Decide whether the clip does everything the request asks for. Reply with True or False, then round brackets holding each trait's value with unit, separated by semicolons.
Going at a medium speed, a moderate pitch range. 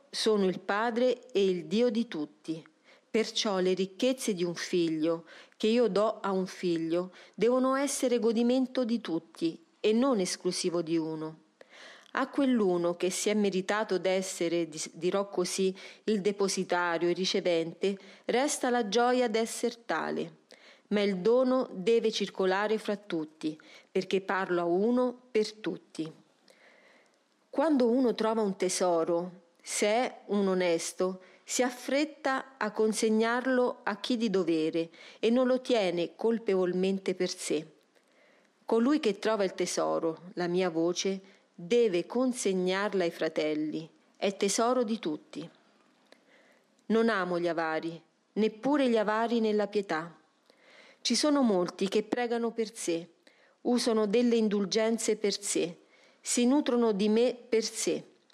True (135 wpm; 4.7 semitones)